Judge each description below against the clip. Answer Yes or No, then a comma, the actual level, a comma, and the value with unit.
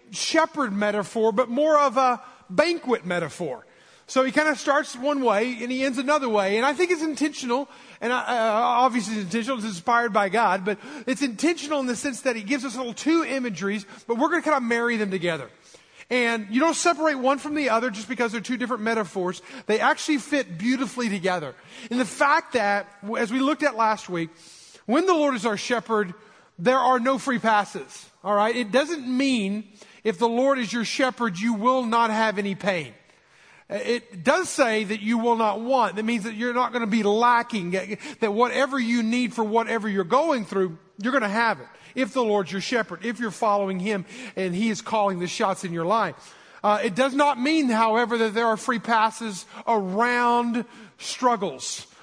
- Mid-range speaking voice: No, high, 235 Hz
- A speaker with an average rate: No, fast, 210 wpm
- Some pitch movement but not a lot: Yes, average, 3.8 semitones